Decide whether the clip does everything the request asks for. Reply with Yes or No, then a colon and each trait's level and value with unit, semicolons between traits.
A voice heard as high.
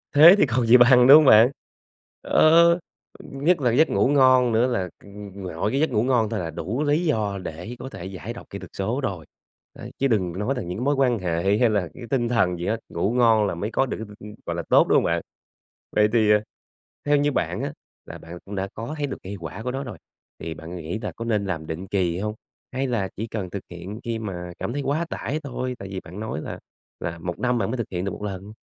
No: low, 110 Hz